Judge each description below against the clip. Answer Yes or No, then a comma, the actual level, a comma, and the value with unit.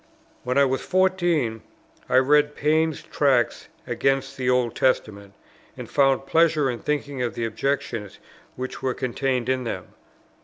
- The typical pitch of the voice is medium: No, low, 130 Hz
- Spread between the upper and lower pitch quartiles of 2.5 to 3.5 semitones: Yes, average, 2.9 semitones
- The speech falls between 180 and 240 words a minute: No, average, 145 wpm